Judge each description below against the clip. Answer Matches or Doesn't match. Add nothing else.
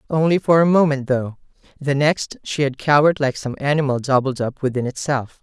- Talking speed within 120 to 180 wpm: Doesn't match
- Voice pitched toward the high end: Doesn't match